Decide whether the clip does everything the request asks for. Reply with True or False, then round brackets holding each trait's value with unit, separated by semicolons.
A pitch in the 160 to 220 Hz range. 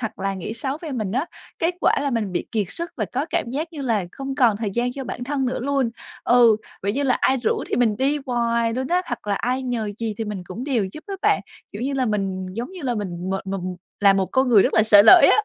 False (235 Hz)